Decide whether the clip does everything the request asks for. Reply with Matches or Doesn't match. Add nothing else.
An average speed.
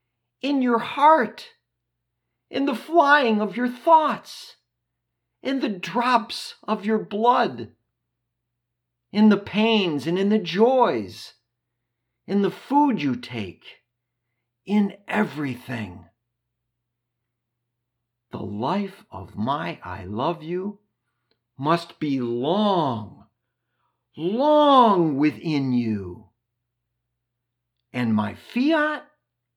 Doesn't match